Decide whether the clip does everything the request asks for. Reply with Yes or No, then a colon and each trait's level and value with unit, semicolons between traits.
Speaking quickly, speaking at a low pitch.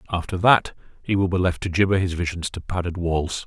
Yes: fast, 225 wpm; very low, 90 Hz